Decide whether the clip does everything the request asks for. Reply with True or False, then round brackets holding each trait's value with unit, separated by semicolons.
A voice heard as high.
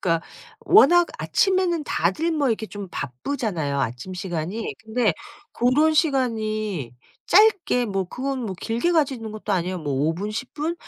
True (220 Hz)